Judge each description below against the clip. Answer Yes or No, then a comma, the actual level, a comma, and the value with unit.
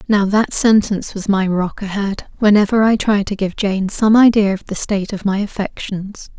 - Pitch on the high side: Yes, high, 200 Hz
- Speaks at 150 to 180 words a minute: No, average, 195 wpm